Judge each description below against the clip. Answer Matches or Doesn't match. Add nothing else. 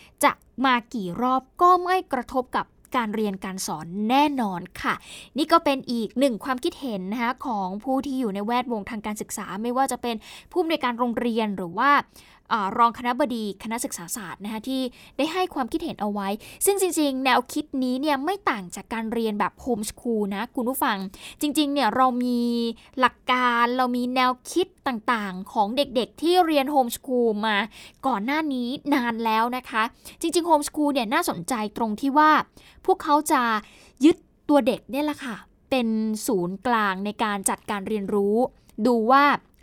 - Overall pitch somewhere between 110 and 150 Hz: Doesn't match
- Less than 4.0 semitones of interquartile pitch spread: Doesn't match